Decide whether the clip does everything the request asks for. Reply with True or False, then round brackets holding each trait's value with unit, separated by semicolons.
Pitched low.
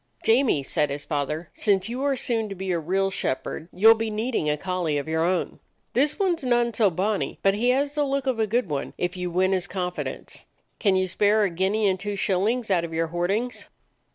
False (195 Hz)